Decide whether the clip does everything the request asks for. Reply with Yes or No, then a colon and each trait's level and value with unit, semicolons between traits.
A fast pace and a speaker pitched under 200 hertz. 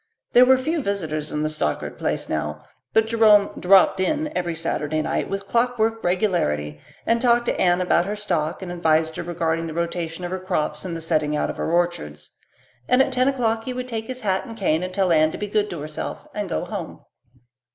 Yes: fast, 215 wpm; medium, 185 Hz